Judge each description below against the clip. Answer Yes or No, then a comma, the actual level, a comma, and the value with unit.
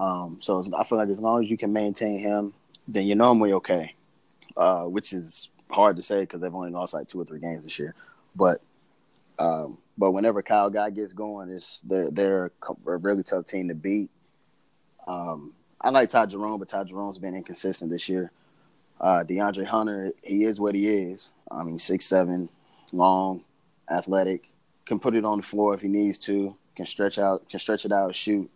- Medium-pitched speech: No, low, 100 Hz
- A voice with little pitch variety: Yes, narrow, 2.0 semitones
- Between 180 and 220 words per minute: Yes, average, 200 wpm